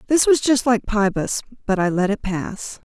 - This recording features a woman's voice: Yes, female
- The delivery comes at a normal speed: Yes, average, 185 wpm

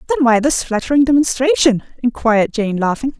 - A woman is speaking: Yes, female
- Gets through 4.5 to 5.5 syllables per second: No, 5.8 syllables/s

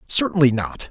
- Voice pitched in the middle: Yes, medium, 145 Hz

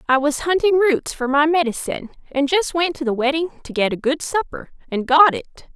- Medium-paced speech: No, fast, 220 wpm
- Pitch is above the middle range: Yes, very high, 295 Hz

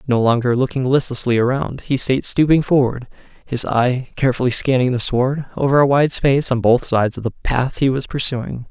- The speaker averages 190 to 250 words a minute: Yes, average, 195 wpm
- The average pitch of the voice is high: No, low, 130 Hz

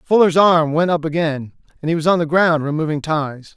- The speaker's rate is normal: No, fast, 220 wpm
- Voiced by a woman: No, male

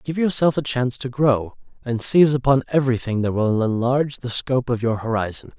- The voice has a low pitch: Yes, low, 125 Hz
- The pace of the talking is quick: No, average, 195 wpm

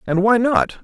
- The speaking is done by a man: Yes, male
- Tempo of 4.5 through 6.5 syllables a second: No, 4.2 syllables/s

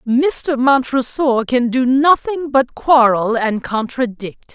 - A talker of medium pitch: No, very high, 255 Hz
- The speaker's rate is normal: No, slow, 120 wpm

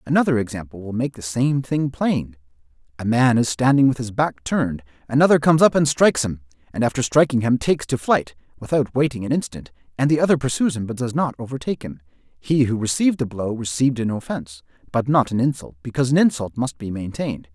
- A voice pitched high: No, low, 125 Hz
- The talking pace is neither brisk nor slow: No, fast, 210 wpm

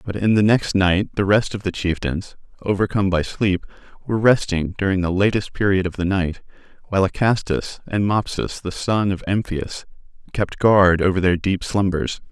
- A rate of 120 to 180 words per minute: Yes, average, 175 wpm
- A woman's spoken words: No, male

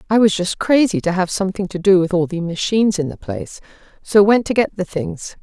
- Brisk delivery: Yes, fast, 245 wpm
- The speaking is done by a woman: Yes, female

